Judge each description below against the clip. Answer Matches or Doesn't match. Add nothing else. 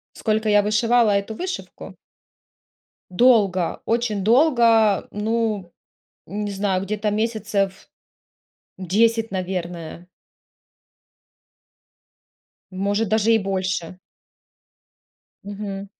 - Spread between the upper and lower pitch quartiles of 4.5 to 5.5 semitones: Doesn't match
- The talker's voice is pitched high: Matches